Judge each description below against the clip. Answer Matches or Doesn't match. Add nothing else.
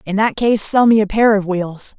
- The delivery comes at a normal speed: Doesn't match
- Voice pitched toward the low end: Doesn't match